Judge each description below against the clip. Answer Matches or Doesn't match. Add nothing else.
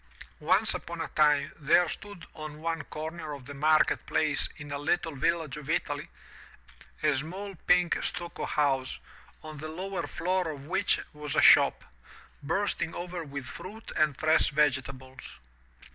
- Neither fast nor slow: Matches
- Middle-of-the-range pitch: Matches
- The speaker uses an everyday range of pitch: Matches